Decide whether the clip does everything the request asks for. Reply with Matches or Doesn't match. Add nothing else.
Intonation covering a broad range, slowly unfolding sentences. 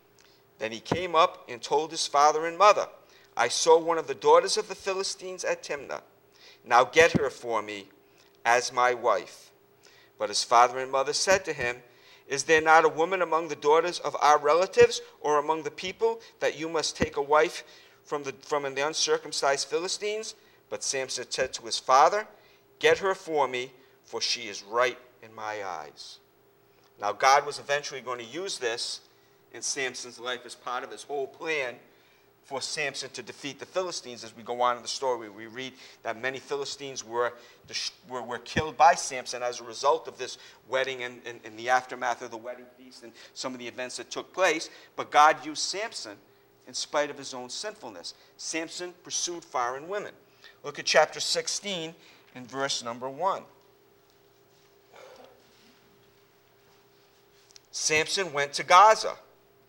Doesn't match